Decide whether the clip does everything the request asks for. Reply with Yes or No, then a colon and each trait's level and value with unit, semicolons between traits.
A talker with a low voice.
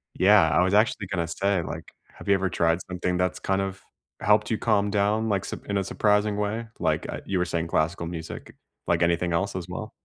Yes: very low, 95 Hz